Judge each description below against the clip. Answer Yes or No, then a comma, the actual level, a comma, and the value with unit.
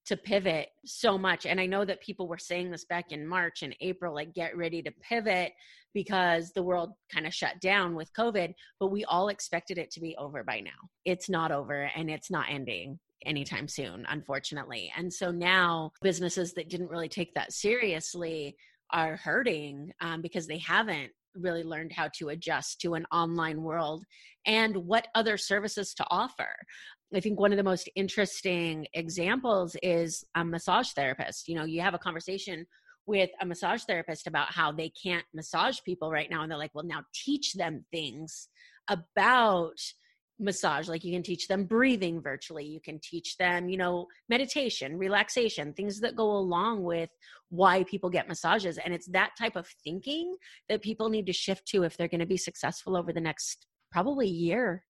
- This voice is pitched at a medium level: Yes, medium, 175 Hz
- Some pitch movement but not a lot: Yes, average, 3.4 semitones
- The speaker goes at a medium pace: Yes, average, 185 wpm